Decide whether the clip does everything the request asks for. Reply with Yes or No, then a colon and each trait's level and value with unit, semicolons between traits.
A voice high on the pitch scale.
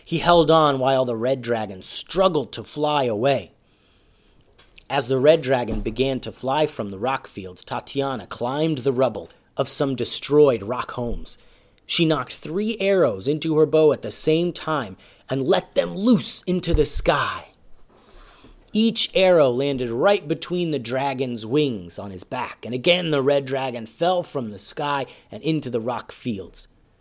No: medium, 140 Hz